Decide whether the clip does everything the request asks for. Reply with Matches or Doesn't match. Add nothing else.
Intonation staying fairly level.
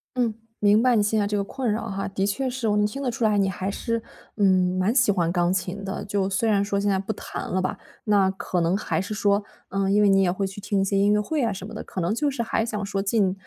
Matches